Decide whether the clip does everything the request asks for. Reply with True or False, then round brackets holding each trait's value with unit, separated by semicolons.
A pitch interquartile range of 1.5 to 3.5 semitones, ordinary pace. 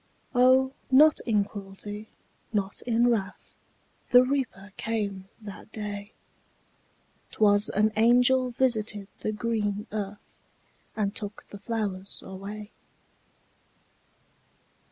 False (2.7 semitones; 95 wpm)